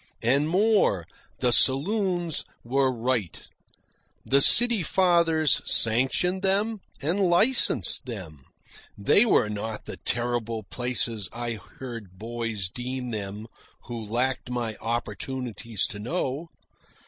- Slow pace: Yes, slow, 110 wpm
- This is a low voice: Yes, low, 125 Hz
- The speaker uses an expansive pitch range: Yes, wide, 6.8 semitones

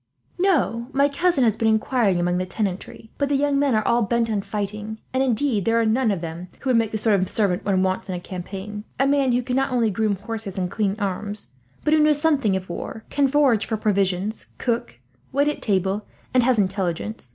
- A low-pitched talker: No, high, 220 Hz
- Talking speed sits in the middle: No, fast, 225 wpm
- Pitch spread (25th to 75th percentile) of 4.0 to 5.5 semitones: Yes, average, 4.8 semitones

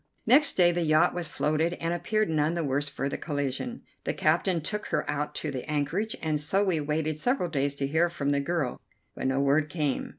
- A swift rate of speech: Yes, fast, 220 wpm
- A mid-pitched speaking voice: Yes, medium, 155 Hz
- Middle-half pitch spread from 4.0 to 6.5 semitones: No, average, 3.3 semitones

